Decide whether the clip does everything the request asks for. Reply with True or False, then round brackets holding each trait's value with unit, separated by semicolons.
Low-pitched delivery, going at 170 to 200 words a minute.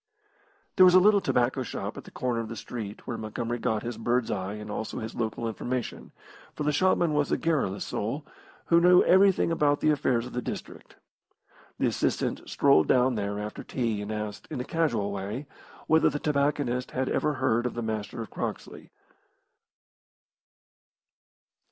True (125 Hz; 175 wpm)